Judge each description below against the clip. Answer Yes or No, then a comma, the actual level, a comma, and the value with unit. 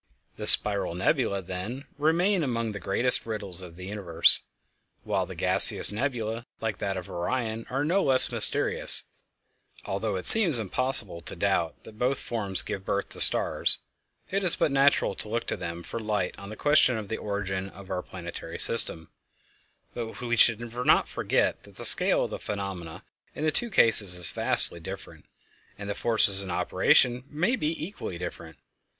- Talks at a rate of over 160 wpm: Yes, average, 175 wpm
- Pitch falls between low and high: No, low, 105 Hz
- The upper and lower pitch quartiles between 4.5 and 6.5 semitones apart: Yes, average, 5.1 semitones